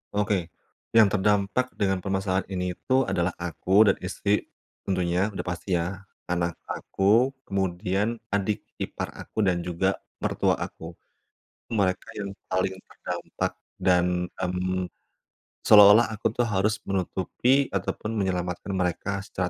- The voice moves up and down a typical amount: No, narrow, 2.3 semitones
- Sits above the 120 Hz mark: No, very low, 95 Hz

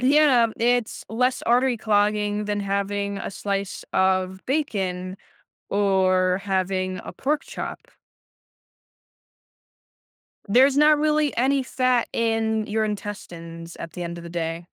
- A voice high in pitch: Yes, high, 205 Hz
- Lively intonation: No, average, 4.7 semitones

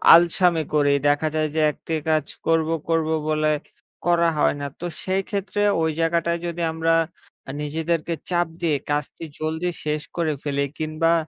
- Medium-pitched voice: Yes, medium, 160 Hz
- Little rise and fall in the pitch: Yes, narrow, 1.7 semitones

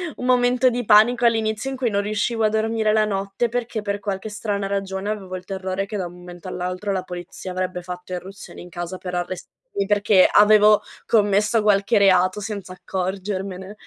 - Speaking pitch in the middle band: No, high, 200 Hz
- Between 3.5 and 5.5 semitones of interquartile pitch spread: No, average, 2.7 semitones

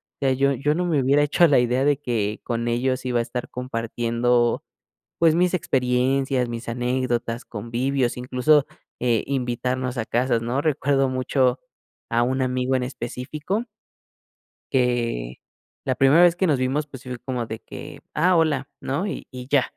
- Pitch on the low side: Yes, low, 130 Hz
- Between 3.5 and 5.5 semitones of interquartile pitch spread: No, narrow, 2.4 semitones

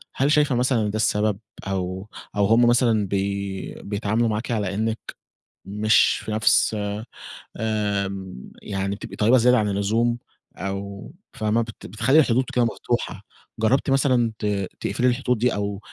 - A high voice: No, low, 110 Hz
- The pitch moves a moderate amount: Yes, average, 3.0 semitones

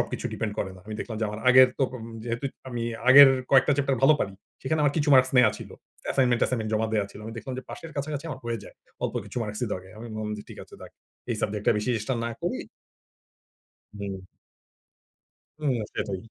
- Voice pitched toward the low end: Yes, low, 120 Hz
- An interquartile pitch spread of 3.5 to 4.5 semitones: Yes, average, 3.9 semitones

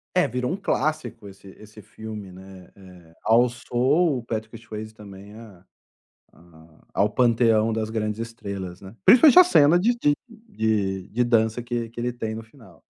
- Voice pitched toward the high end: No, low, 110 Hz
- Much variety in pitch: No, average, 3.6 semitones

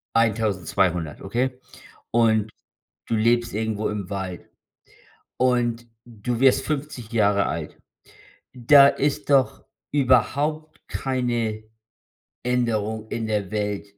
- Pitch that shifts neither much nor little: Yes, average, 3.3 semitones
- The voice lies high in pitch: No, low, 115 Hz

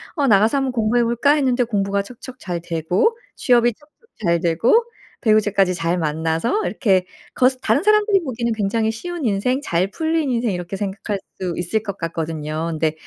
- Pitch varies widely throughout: Yes, wide, 6.3 semitones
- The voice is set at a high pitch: Yes, high, 215 Hz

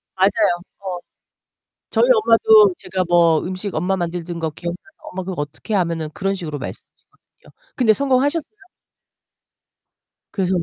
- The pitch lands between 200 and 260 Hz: No, high, 190 Hz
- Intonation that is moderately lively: Yes, average, 4.2 semitones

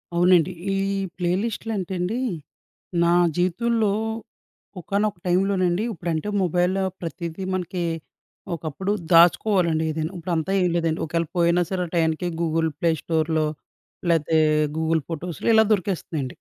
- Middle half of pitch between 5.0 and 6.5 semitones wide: No, narrow, 2.4 semitones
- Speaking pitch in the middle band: Yes, medium, 175 Hz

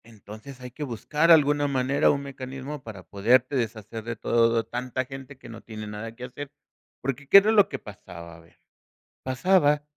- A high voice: No, low, 130 Hz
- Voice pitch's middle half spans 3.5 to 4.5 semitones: Yes, average, 3.9 semitones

